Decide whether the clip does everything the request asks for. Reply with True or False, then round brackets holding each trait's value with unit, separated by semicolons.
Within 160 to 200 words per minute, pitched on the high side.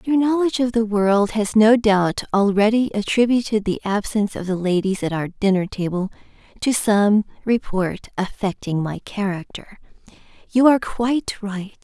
False (145 wpm; 210 Hz)